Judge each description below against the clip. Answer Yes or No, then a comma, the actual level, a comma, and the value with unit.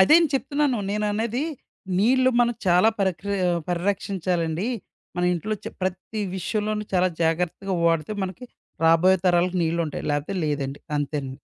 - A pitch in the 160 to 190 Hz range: Yes, medium, 185 Hz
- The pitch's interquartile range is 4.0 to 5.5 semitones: Yes, average, 4.3 semitones